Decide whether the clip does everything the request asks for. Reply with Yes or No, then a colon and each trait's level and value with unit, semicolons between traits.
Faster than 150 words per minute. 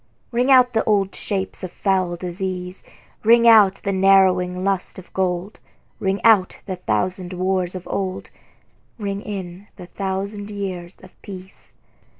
No: average, 140 wpm